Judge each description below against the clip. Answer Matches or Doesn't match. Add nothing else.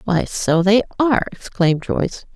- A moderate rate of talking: Matches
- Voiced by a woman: Matches